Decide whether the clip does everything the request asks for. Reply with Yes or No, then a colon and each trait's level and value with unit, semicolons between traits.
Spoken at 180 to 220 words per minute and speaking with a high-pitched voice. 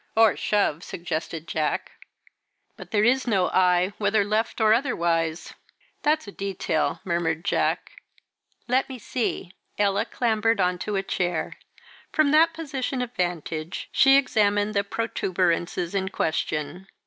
No: slow, 135 wpm; high, 200 Hz